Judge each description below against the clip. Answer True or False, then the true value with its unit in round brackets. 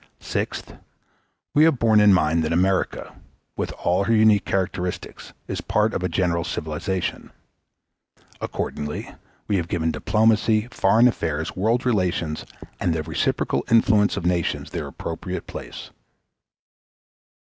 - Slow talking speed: True (130 wpm)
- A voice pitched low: True (95 Hz)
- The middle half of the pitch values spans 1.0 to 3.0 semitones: False (4.4 semitones)